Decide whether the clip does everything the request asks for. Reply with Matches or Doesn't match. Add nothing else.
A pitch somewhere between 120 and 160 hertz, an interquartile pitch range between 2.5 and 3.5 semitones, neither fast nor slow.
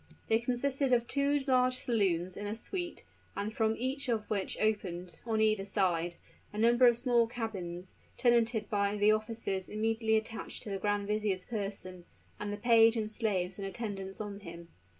Doesn't match